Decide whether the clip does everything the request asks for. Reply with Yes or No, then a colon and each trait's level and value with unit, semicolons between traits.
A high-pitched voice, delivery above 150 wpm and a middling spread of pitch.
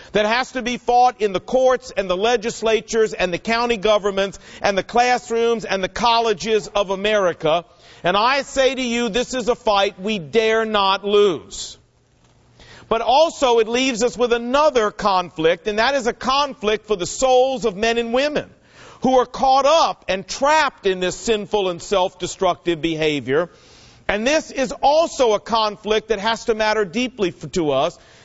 Yes: high, 220 Hz; average, 175 wpm; average, 3.9 semitones